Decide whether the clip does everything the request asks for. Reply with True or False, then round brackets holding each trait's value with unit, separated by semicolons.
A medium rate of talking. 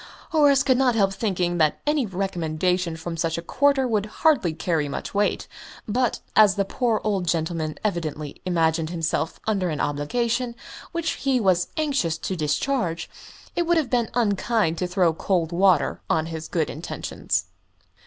True (160 wpm)